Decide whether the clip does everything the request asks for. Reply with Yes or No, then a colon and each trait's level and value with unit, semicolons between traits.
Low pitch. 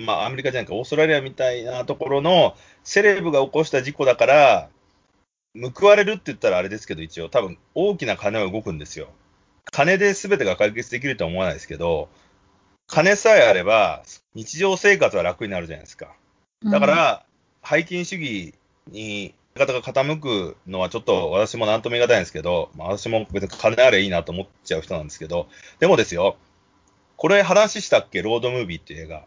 Yes: low, 125 Hz